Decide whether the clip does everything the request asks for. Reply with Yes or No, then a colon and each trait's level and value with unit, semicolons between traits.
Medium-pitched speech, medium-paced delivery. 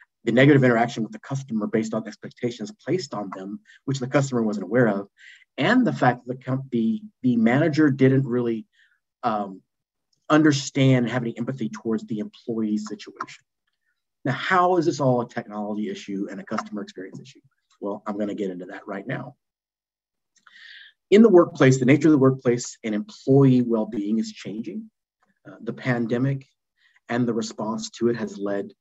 No: low, 120 Hz; average, 175 wpm